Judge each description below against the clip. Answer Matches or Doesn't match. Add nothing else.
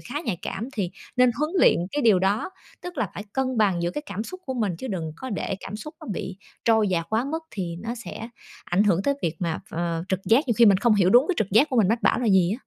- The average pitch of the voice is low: Doesn't match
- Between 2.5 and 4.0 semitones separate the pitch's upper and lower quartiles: Doesn't match